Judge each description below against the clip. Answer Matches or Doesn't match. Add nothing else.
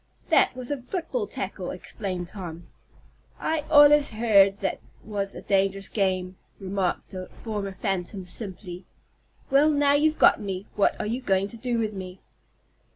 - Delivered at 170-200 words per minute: Doesn't match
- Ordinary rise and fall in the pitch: Matches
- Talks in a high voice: Matches